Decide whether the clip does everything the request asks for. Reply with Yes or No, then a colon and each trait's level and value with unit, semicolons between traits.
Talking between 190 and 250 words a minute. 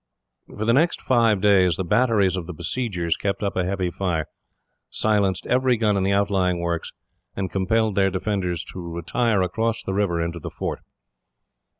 No: average, 175 wpm